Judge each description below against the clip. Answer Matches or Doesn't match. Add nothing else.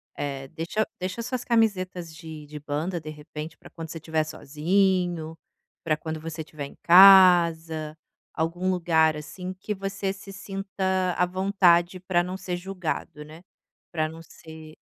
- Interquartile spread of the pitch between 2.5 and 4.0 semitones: Matches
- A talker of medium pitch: Matches